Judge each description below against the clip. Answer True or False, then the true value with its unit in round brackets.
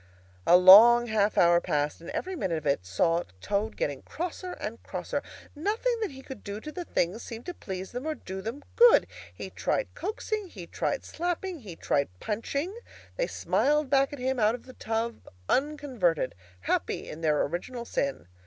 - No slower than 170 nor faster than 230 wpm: True (180 wpm)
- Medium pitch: False (235 Hz)